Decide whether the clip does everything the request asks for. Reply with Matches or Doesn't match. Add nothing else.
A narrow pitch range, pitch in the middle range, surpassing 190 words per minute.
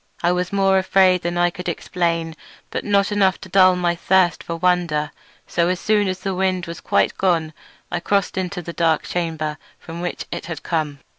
Matches